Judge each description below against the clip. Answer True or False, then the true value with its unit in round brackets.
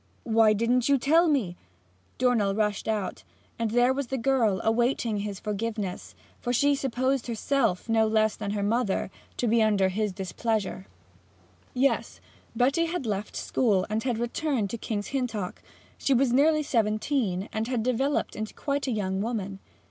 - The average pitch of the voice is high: True (225 Hz)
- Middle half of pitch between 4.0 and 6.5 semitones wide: False (3.6 semitones)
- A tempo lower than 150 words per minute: False (160 wpm)